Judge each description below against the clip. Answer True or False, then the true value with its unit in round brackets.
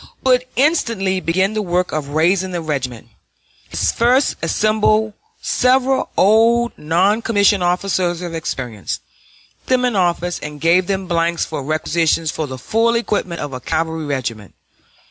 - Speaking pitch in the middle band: True (180 Hz)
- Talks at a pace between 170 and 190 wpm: False (145 wpm)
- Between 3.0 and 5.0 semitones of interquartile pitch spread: False (5.4 semitones)